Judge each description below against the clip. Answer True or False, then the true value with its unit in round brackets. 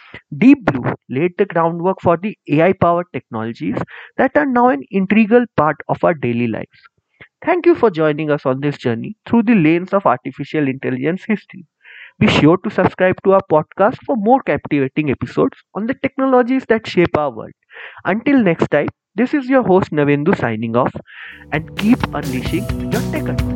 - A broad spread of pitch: True (7.5 semitones)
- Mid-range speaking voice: True (175 Hz)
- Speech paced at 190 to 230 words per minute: False (175 wpm)